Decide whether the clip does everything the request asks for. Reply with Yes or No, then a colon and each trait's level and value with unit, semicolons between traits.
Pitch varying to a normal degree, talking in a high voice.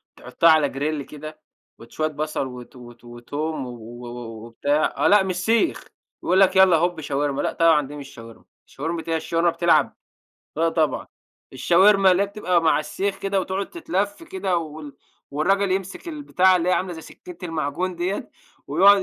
No: average, 4.6 semitones; medium, 165 Hz